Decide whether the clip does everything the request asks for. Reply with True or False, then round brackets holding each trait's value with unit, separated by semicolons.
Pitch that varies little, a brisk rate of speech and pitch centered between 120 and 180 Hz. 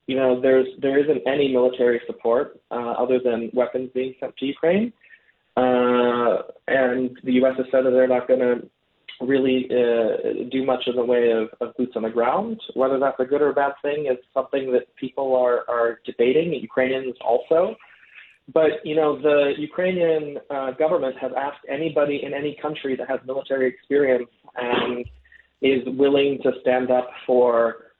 False (2.2 semitones; 175 wpm; 130 Hz)